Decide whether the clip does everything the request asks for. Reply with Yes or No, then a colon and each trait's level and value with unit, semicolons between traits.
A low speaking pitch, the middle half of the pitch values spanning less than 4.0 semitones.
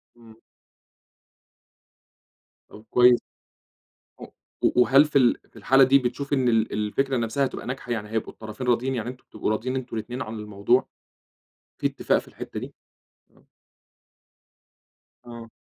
Yes: low, 120 Hz; average, 2.8 semitones